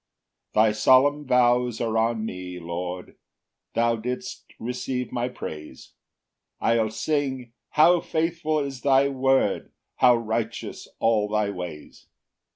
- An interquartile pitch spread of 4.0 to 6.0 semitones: No, average, 3.6 semitones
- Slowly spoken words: Yes, slow, 120 wpm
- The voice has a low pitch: Yes, low, 120 Hz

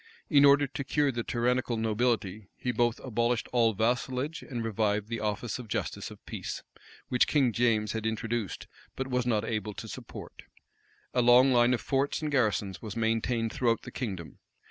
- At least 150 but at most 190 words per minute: Yes, average, 175 wpm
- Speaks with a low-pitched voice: Yes, low, 120 Hz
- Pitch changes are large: No, narrow, 2.5 semitones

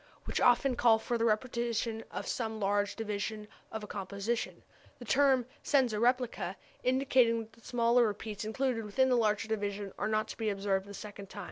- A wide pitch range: No, narrow, 2.6 semitones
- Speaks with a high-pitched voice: Yes, high, 225 Hz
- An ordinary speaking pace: Yes, average, 180 wpm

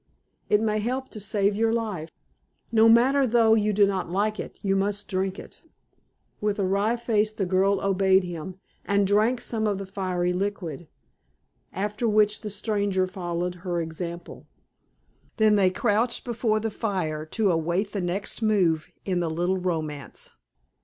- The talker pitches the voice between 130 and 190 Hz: No, high, 200 Hz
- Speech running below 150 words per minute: No, average, 160 wpm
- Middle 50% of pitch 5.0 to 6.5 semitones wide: No, average, 3.0 semitones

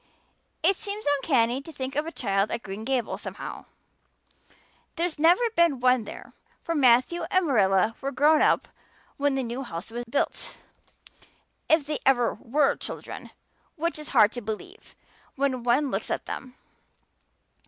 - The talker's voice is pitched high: Yes, very high, 270 Hz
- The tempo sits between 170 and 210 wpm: No, average, 155 wpm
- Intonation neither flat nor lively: Yes, average, 4.7 semitones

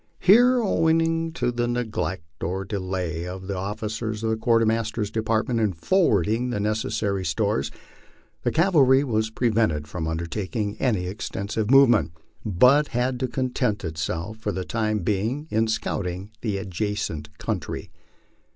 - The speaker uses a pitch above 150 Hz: No, low, 110 Hz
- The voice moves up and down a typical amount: Yes, average, 4.4 semitones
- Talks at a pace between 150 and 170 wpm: No, slow, 135 wpm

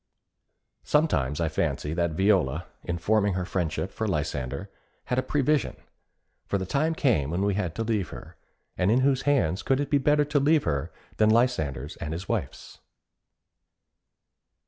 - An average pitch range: No, wide, 8.4 semitones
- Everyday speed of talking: Yes, average, 165 wpm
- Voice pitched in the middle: No, low, 100 Hz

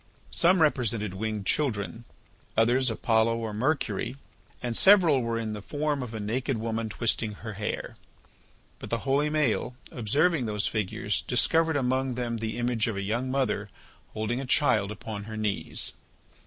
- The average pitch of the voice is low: Yes, low, 115 Hz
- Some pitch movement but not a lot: Yes, average, 3.6 semitones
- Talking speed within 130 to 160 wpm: Yes, average, 155 wpm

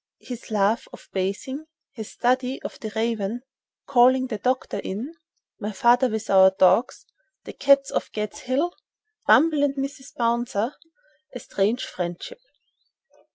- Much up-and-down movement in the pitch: No, average, 4.6 semitones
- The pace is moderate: No, slow, 110 wpm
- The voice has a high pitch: Yes, very high, 250 Hz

